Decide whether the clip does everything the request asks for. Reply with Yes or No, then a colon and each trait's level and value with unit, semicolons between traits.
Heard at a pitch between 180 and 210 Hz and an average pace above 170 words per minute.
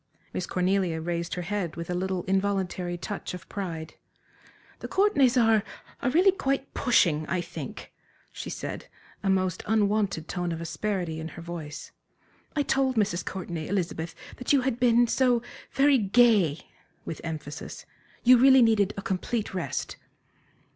No: high, 190 Hz; average, 150 wpm